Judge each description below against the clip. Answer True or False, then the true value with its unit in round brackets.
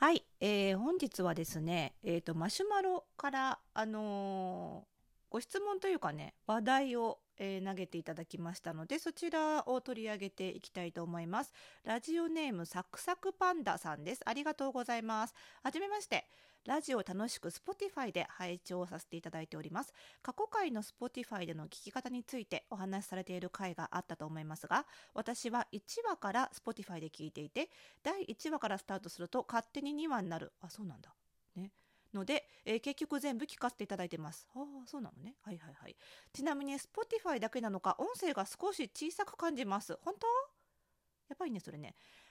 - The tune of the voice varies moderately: False (8.4 semitones)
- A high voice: True (225 Hz)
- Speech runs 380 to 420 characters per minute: True (400 characters per minute)